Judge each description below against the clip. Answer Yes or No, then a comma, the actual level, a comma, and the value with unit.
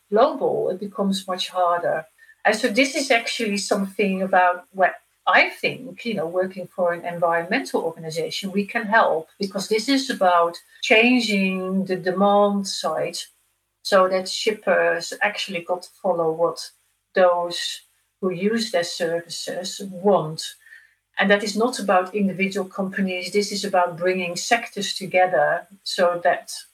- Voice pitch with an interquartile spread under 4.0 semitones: Yes, average, 3.0 semitones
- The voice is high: Yes, high, 195 Hz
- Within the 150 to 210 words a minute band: No, average, 140 wpm